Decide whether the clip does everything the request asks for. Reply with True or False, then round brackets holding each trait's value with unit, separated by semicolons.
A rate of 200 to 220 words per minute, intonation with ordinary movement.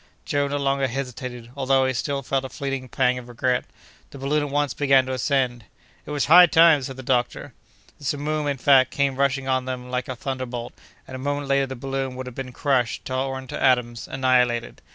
False (205 wpm; 1.6 semitones)